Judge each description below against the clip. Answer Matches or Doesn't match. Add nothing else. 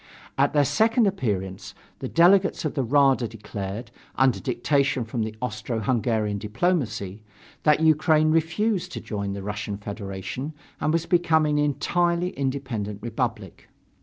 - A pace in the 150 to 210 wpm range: Doesn't match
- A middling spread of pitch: Doesn't match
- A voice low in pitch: Matches